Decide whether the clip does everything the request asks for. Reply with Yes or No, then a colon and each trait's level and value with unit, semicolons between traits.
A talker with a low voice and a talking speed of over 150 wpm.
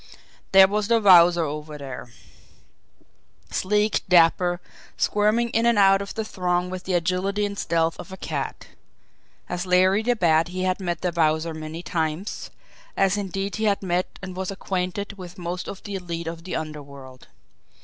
No: medium, 180 Hz; average, 170 wpm